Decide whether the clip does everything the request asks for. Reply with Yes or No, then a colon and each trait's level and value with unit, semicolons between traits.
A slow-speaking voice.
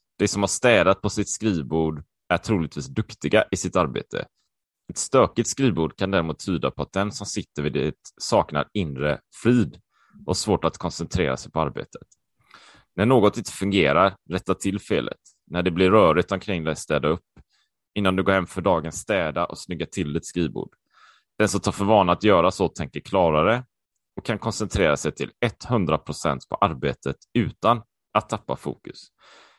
No: average, 170 wpm